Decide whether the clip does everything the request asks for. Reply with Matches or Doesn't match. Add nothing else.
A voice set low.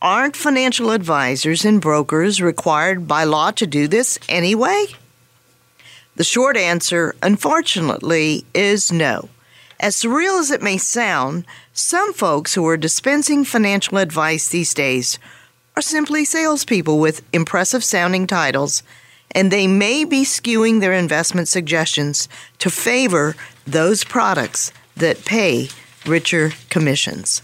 Doesn't match